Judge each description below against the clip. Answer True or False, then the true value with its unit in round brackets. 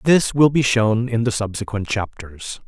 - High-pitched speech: False (115 Hz)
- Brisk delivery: False (180 wpm)